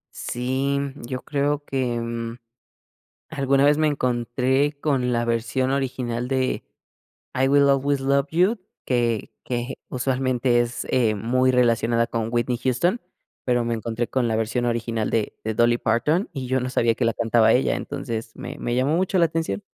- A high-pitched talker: No, low, 125 Hz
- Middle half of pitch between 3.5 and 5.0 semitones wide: No, average, 2.7 semitones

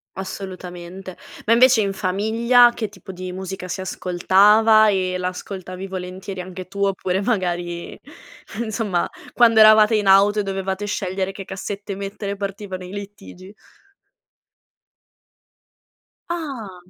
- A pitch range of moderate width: No, narrow, 2.1 semitones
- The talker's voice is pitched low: No, high, 195 Hz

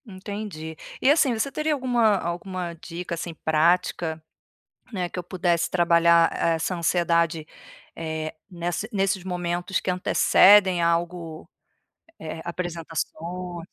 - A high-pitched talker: No, medium, 175 Hz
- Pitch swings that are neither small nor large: No, narrow, 2.0 semitones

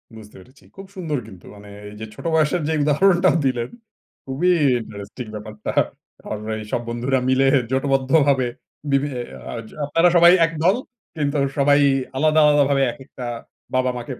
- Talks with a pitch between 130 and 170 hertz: Yes, low, 135 Hz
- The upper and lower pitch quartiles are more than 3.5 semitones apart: Yes, average, 4.2 semitones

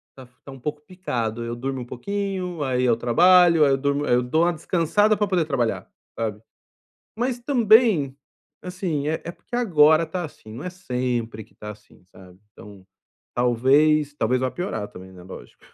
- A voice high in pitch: No, medium, 145 Hz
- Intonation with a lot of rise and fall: Yes, wide, 7.0 semitones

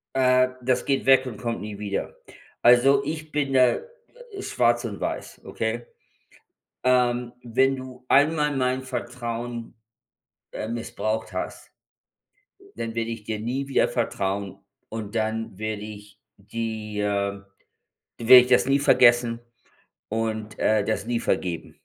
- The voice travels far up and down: No, average, 2.8 semitones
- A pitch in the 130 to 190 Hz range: No, low, 120 Hz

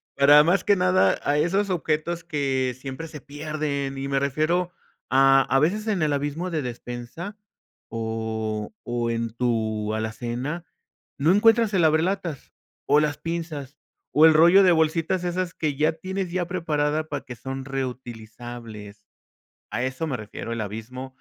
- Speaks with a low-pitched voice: No, medium, 145 Hz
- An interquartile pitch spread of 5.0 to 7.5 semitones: Yes, wide, 5.5 semitones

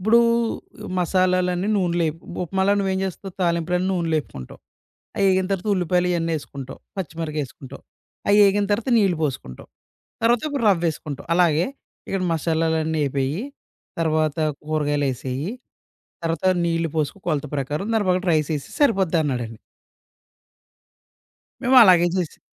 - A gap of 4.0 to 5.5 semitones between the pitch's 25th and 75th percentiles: No, average, 3.6 semitones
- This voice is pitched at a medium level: Yes, medium, 170 Hz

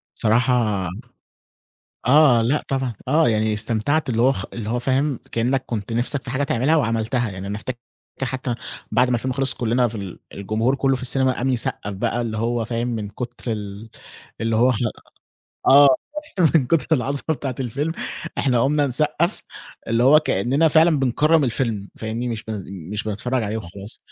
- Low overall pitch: Yes, low, 120 Hz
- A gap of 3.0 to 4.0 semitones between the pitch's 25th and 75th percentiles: Yes, average, 3.4 semitones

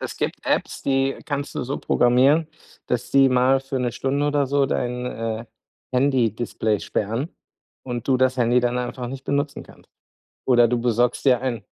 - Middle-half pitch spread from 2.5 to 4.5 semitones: No, narrow, 2.0 semitones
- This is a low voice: Yes, low, 125 Hz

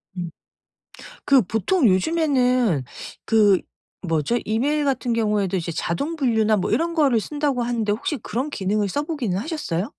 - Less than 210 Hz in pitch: No, high, 230 Hz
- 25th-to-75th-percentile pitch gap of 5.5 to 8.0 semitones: Yes, wide, 6.3 semitones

